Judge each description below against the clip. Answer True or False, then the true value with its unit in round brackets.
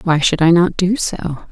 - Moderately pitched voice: True (170 Hz)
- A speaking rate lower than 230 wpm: False (240 wpm)